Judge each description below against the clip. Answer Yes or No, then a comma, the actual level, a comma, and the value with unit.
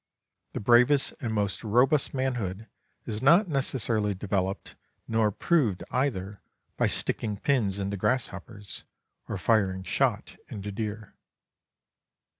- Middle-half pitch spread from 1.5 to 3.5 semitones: No, average, 4.3 semitones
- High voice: No, low, 110 Hz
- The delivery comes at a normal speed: No, slow, 110 wpm